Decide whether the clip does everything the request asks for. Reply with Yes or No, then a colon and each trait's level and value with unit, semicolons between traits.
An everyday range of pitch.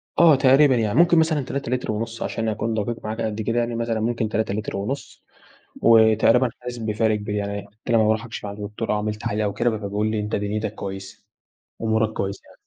No: narrow, 2.0 semitones